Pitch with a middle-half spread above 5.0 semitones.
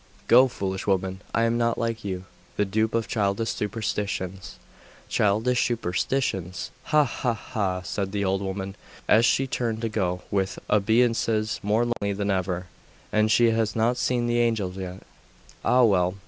No: average, 3.2 semitones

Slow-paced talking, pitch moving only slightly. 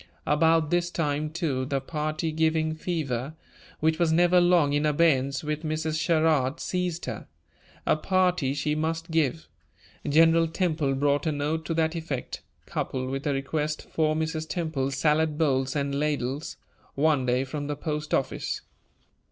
No: average, 150 wpm; narrow, 2.3 semitones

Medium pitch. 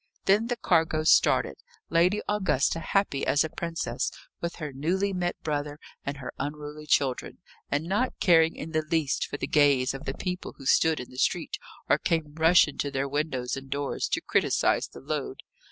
Yes: medium, 155 Hz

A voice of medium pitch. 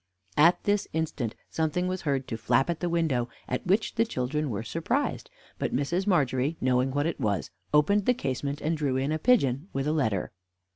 Yes: medium, 150 Hz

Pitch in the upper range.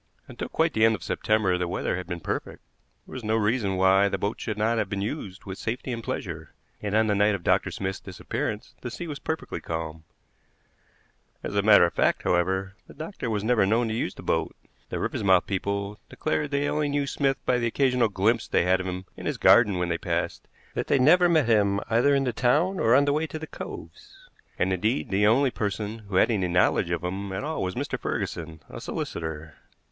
No: low, 105 Hz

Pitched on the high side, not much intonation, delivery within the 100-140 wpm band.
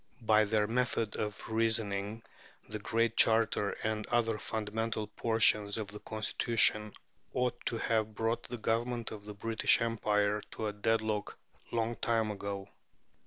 No: low, 110 Hz; narrow, 1.4 semitones; slow, 135 wpm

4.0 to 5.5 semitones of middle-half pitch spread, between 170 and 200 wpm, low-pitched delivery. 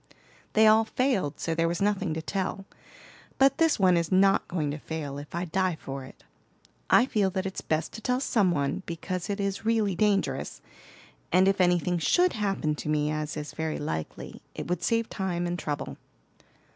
No: average, 4.3 semitones; average, 190 wpm; medium, 185 Hz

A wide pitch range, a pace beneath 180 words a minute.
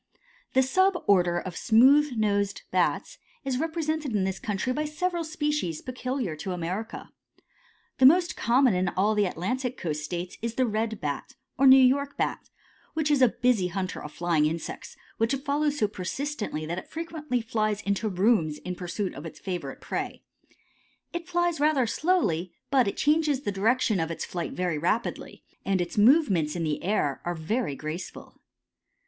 Yes: wide, 7.7 semitones; average, 170 wpm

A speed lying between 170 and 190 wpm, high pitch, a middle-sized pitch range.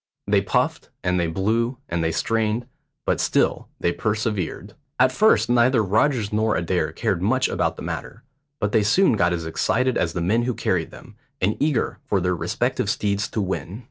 No: average, 185 wpm; low, 105 Hz; average, 4.6 semitones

